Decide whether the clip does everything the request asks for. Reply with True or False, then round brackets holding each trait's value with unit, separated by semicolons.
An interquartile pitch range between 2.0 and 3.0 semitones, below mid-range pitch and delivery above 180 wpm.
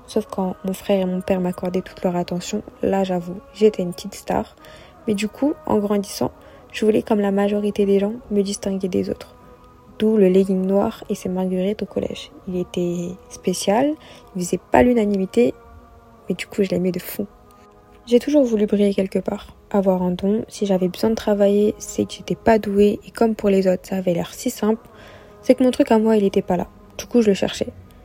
False (2.6 semitones; 200 Hz; 215 wpm)